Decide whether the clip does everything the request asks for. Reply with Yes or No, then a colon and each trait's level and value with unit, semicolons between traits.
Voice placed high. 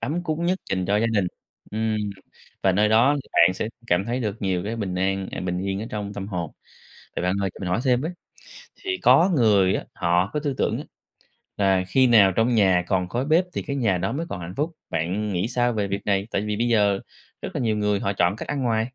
No: low, 105 Hz